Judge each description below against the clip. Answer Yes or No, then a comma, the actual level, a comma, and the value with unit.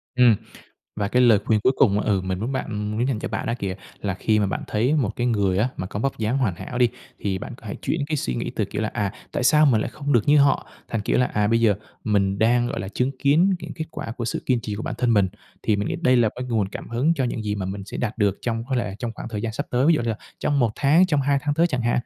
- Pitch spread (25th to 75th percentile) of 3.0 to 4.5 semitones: Yes, average, 3.8 semitones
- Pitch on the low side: Yes, low, 115 Hz